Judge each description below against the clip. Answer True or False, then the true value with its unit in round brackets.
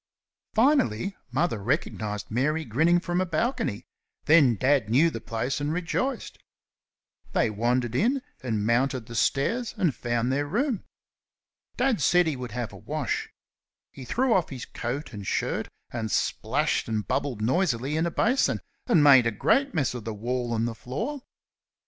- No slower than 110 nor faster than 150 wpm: False (160 wpm)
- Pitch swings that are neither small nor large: False (7.0 semitones)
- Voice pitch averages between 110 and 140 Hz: True (135 Hz)